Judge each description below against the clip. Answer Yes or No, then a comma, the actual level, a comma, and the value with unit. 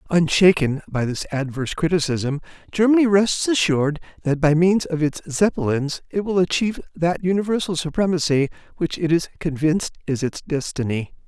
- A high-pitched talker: No, medium, 165 Hz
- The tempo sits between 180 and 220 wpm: No, average, 145 wpm